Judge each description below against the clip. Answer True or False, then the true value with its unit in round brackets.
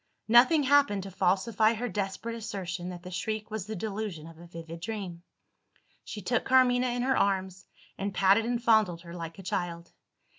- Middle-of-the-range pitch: False (200 Hz)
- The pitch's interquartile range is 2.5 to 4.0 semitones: False (4.4 semitones)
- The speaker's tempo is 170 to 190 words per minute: True (180 wpm)